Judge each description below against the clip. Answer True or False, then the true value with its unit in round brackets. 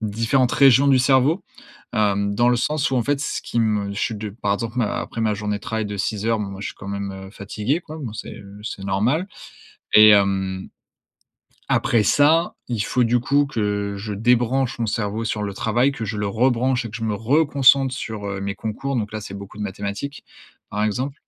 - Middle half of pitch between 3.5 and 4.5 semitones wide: True (3.9 semitones)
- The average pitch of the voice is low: True (110 Hz)